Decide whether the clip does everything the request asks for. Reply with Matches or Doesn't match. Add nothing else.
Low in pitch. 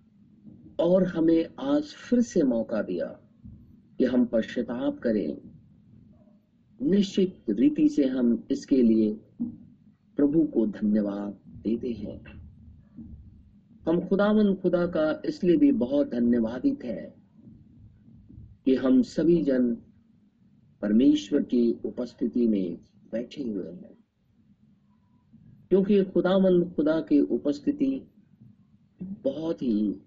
Doesn't match